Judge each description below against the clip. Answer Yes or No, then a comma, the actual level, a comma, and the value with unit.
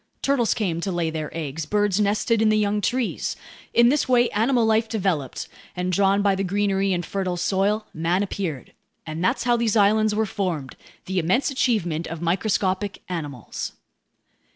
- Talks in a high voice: Yes, high, 195 Hz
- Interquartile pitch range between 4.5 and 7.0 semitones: No, average, 3.9 semitones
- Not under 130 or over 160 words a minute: No, average, 170 wpm